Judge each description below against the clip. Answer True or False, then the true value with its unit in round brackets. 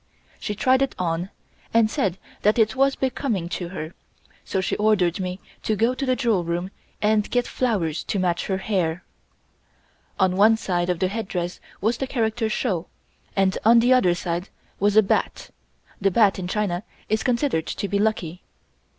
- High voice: True (200 Hz)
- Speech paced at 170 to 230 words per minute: True (180 wpm)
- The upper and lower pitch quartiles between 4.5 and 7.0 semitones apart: False (3.9 semitones)